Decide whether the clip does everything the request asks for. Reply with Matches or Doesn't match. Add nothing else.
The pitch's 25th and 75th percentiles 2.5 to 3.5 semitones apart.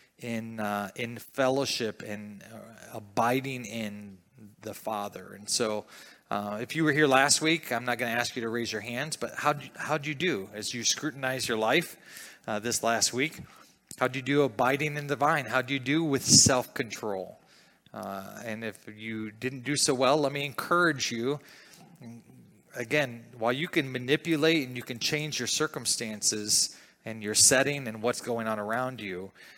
Doesn't match